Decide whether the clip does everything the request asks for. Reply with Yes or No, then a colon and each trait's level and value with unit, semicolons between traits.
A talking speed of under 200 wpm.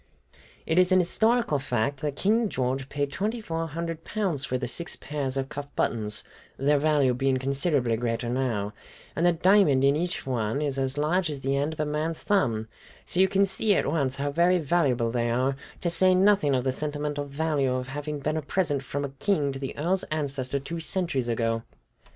No: fast, 205 wpm